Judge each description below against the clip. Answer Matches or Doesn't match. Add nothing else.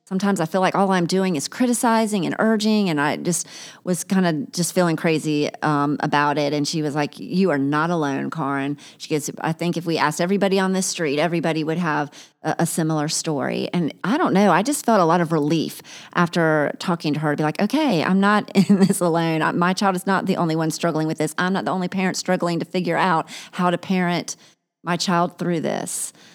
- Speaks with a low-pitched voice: Doesn't match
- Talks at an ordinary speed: Doesn't match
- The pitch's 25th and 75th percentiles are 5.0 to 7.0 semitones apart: Doesn't match